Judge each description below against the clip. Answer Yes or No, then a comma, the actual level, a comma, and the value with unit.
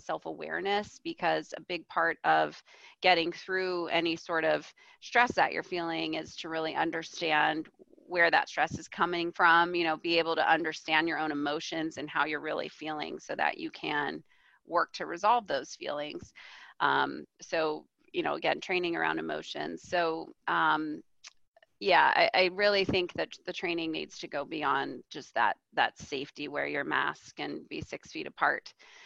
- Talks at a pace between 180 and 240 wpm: No, average, 170 wpm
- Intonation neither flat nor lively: Yes, average, 3.7 semitones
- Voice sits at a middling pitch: Yes, medium, 170 Hz